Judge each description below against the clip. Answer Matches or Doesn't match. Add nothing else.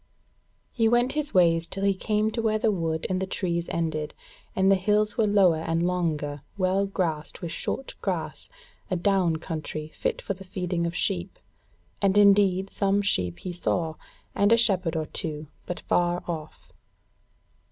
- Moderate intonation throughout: Matches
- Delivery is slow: Doesn't match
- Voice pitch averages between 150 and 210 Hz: Matches